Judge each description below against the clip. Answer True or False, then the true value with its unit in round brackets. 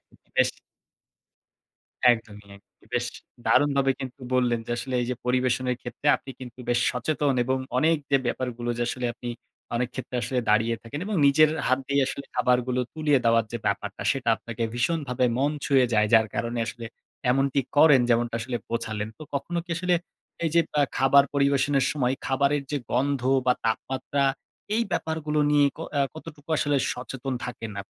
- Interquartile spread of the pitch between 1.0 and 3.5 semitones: True (2.9 semitones)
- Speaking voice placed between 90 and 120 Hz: False (130 Hz)